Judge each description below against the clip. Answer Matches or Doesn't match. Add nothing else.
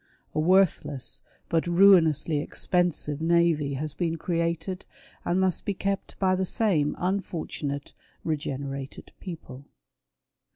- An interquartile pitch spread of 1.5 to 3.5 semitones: Doesn't match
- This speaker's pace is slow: Matches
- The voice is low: Doesn't match